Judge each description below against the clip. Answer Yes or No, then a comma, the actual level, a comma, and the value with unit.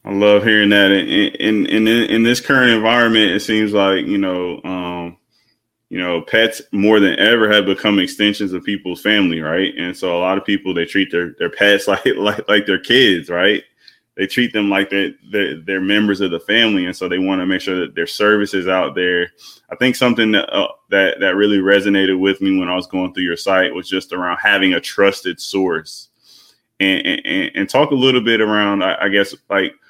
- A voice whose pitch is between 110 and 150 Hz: No, low, 100 Hz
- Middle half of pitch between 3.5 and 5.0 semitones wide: No, narrow, 2.5 semitones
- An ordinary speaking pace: No, fast, 215 wpm